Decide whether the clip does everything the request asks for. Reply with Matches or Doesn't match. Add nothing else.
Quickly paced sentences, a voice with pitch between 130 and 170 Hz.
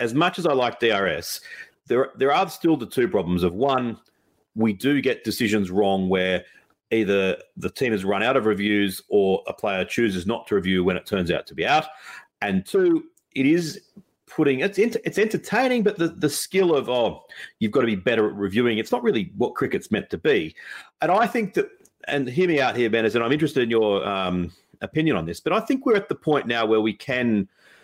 Matches